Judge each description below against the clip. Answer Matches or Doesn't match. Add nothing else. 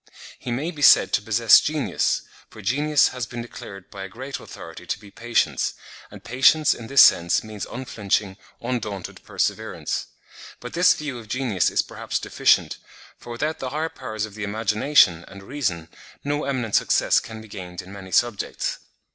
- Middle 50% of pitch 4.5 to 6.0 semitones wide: Matches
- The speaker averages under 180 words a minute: Matches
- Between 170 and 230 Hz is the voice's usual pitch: Doesn't match